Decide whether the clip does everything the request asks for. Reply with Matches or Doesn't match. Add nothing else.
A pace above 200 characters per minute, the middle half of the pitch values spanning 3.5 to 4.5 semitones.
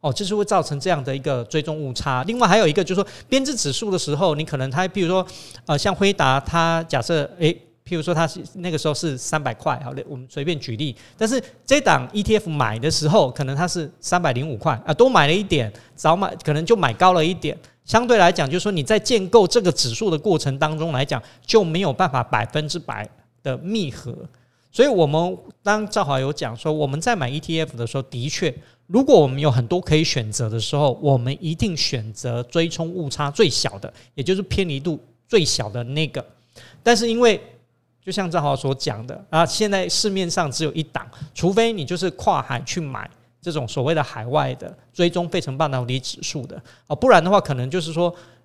Doesn't match